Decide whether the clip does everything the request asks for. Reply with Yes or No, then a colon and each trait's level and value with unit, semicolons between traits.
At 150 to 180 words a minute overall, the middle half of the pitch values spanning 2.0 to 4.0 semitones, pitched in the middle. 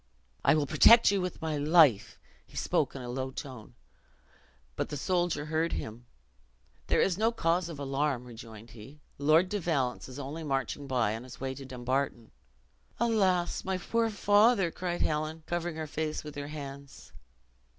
No: average, 170 wpm; average, 4.8 semitones; medium, 150 Hz